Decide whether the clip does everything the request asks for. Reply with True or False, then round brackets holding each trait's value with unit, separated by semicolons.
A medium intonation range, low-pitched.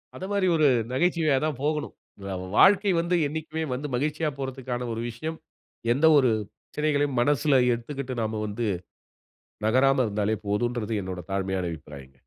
False (5.8 semitones; 130 Hz)